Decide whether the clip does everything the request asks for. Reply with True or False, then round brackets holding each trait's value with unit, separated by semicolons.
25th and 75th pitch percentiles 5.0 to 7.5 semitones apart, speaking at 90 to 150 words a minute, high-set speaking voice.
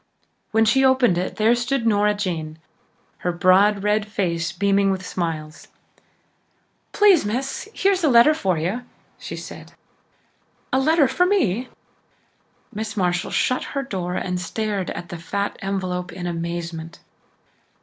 True (5.3 semitones; 140 wpm; 200 Hz)